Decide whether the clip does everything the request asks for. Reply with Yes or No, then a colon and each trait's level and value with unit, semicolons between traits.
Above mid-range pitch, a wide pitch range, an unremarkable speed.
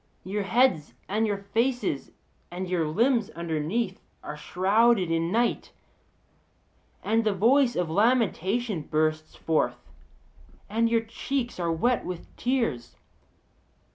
No: high, 200 Hz; wide, 5.9 semitones; slow, 115 wpm